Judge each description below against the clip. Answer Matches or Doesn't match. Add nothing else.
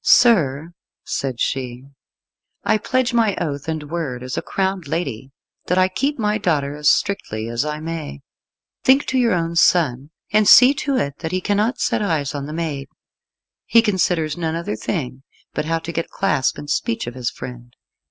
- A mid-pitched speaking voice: Matches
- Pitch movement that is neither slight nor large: Doesn't match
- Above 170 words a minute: Matches